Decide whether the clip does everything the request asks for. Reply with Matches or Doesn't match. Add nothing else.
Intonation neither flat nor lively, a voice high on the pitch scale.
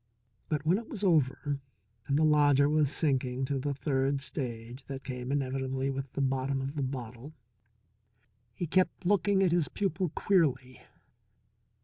Doesn't match